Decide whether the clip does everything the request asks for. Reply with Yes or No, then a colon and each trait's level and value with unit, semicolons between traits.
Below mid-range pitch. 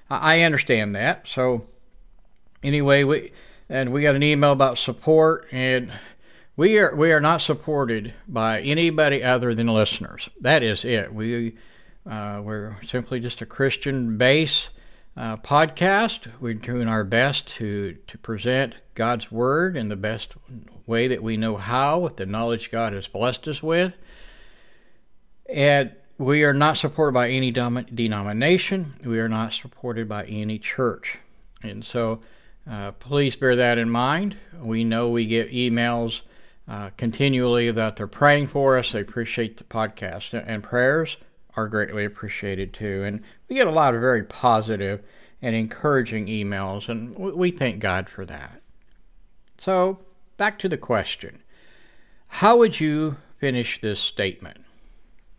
Yes: low, 120 Hz